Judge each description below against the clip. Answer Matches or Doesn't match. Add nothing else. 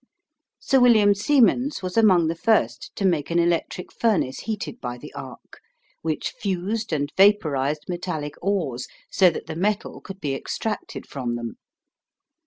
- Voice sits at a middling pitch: Matches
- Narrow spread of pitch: Doesn't match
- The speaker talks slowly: Doesn't match